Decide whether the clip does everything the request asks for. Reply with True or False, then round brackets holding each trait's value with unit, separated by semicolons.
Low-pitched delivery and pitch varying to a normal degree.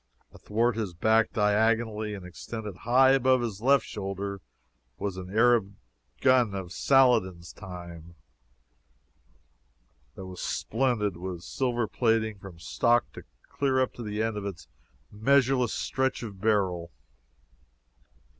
True (110 Hz; 4.0 semitones)